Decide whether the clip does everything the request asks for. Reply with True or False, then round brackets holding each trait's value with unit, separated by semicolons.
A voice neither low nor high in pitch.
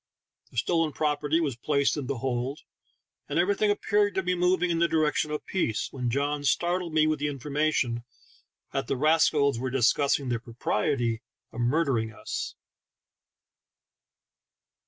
True (145 Hz)